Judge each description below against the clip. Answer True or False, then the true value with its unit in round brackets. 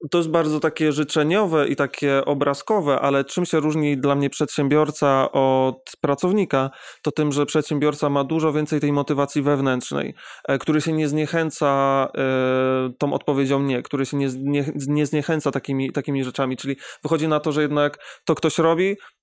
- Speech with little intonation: True (1.9 semitones)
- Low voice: False (145 Hz)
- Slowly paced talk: False (155 wpm)